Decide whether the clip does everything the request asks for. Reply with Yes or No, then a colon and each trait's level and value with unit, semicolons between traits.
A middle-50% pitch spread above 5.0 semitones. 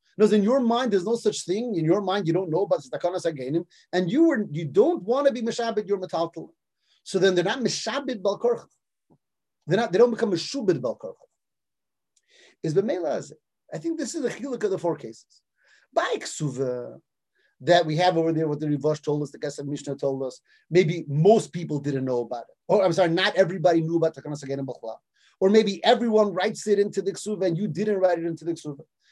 Yes: wide, 5.4 semitones